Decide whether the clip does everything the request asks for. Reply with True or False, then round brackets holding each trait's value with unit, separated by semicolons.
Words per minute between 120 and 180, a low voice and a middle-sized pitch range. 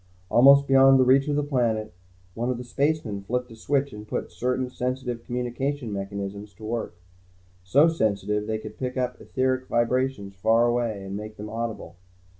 True (170 wpm; 120 Hz; 3.5 semitones)